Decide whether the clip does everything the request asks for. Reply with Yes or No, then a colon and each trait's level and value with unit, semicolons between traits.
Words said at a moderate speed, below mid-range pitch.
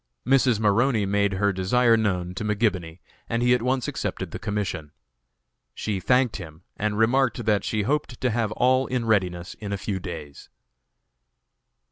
Yes: average, 160 wpm; low, 105 Hz